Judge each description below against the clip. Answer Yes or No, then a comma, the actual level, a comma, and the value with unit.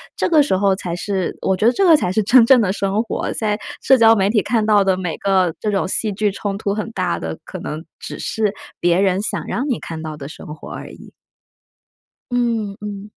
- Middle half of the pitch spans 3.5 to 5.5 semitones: No, average, 3.0 semitones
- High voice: Yes, high, 200 Hz